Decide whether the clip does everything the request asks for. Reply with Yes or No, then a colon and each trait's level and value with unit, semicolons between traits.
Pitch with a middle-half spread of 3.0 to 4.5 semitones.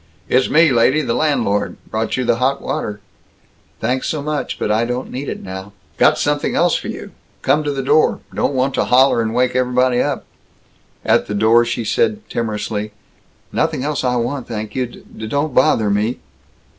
Yes: average, 3.6 semitones